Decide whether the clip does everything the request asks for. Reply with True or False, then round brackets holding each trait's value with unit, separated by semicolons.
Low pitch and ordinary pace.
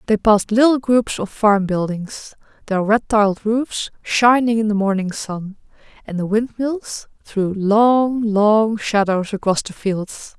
False (215 Hz; 150 wpm)